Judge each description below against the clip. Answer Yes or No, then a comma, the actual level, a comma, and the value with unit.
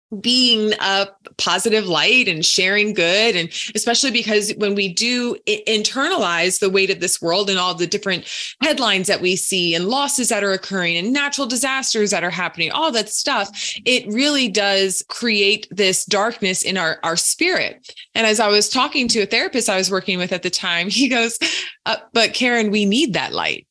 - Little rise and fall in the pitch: No, average, 4.1 semitones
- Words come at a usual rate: Yes, average, 190 wpm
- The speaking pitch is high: Yes, high, 210 Hz